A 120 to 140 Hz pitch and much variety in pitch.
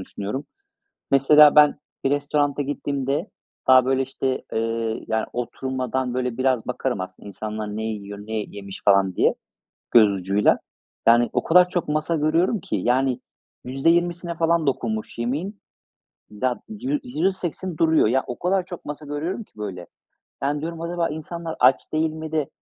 Yes: low, 135 Hz; wide, 5.9 semitones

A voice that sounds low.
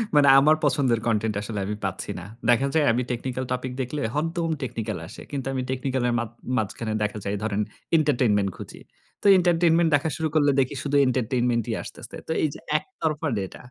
Yes: low, 130 Hz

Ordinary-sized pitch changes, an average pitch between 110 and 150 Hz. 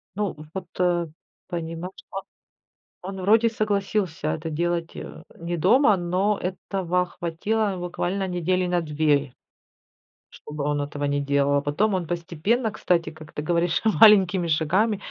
No: average, 3.4 semitones; medium, 175 Hz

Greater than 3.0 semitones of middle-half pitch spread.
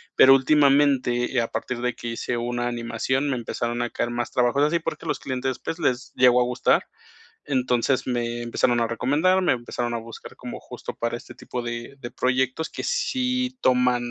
No: narrow, 2.6 semitones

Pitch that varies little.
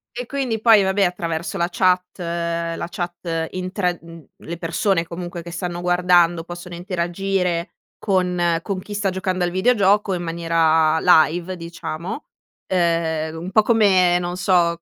Yes: narrow, 1.8 semitones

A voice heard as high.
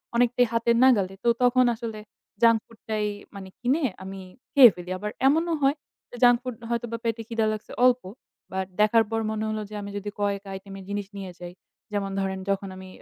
Yes: high, 215 Hz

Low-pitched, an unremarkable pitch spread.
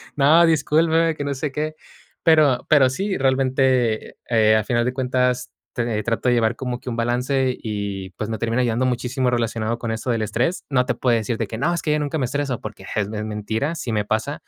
Yes: low, 125 Hz; average, 3.6 semitones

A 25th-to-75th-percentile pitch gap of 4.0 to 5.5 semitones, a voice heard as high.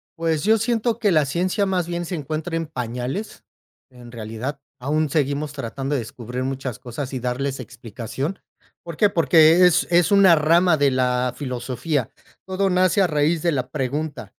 No: average, 5.2 semitones; medium, 150 Hz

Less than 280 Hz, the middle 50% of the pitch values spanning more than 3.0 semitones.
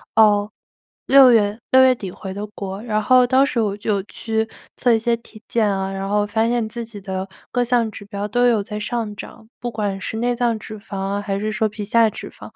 No: high, 215 Hz; narrow, 2.5 semitones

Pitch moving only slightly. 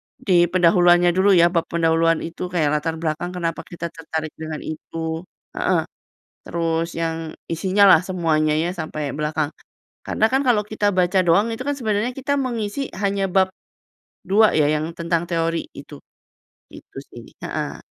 No: average, 3.1 semitones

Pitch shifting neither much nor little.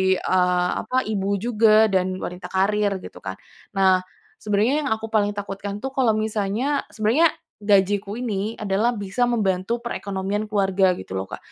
No: narrow, 2.3 semitones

